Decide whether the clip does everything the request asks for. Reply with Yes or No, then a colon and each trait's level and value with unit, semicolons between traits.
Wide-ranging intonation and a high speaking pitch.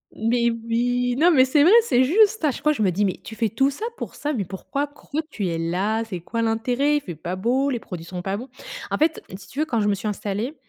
Yes: wide, 5.7 semitones; high, 235 Hz